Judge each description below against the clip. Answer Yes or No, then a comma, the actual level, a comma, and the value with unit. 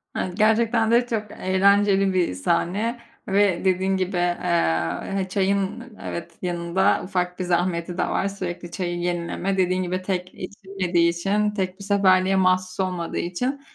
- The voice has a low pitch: No, medium, 185 Hz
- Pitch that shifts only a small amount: Yes, narrow, 2.0 semitones